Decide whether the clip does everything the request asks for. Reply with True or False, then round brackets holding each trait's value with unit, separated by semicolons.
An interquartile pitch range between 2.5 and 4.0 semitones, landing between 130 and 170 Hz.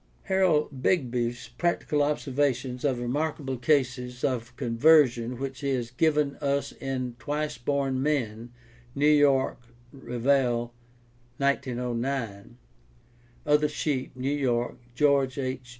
True (2.9 semitones; 135 Hz)